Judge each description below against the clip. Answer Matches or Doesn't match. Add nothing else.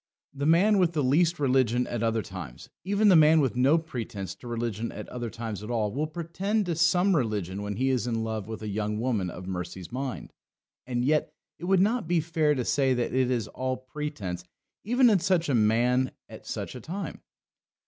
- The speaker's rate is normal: Doesn't match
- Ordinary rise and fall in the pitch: Doesn't match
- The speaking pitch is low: Matches